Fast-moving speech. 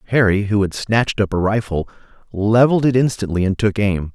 No: average, 190 wpm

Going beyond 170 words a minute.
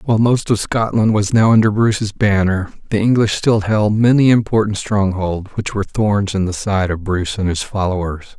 Yes: average, 195 wpm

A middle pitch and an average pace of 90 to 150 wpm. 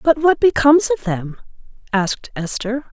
No: very high, 255 Hz; average, 140 wpm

